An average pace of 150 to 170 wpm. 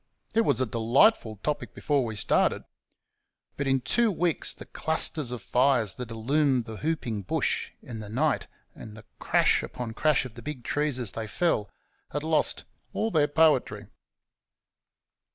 Yes: average, 160 wpm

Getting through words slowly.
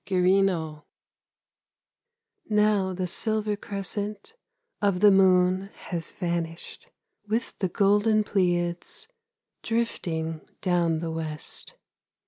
Yes: slow, 90 wpm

